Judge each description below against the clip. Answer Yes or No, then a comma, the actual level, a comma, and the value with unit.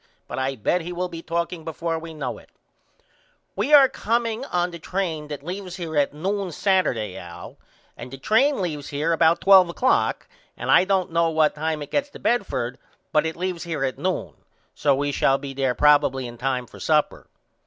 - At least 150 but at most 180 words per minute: No, average, 195 wpm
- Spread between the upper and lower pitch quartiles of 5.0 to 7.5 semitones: No, average, 4.3 semitones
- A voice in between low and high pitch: Yes, medium, 165 Hz